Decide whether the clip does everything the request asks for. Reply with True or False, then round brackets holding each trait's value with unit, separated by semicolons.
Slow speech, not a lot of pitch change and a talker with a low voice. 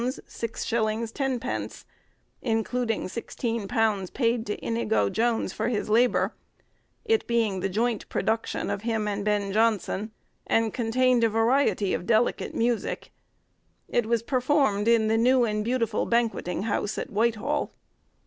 False (130 wpm; 2.2 semitones; 225 Hz)